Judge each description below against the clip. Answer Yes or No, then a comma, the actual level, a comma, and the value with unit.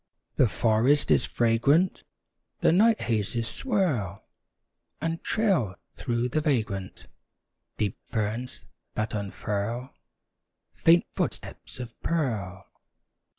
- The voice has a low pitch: Yes, low, 120 Hz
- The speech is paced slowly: Yes, slow, 95 wpm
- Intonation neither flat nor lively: No, wide, 6.7 semitones